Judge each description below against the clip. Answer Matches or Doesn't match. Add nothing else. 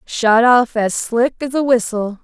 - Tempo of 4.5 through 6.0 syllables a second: Doesn't match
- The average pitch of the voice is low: Doesn't match